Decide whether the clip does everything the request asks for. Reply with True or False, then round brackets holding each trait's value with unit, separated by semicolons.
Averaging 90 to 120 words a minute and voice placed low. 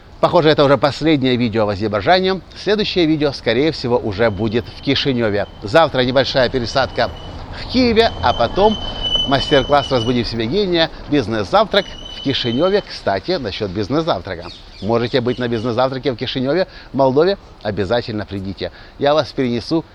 False (135 wpm; 130 Hz)